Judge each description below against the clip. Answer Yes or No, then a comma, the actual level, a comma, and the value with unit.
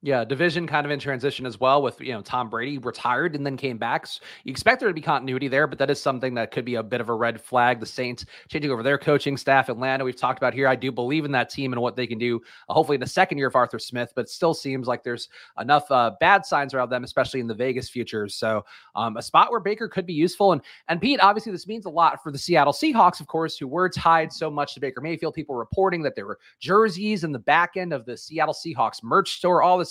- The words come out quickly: Yes, fast, 275 wpm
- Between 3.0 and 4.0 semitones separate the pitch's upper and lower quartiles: No, average, 4.8 semitones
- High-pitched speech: No, medium, 140 Hz